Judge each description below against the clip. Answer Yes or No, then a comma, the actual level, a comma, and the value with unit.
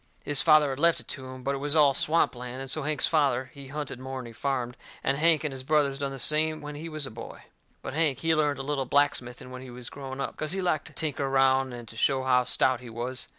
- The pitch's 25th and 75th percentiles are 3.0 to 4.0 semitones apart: No, narrow, 2.6 semitones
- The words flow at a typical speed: No, fast, 270 wpm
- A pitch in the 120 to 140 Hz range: Yes, low, 135 Hz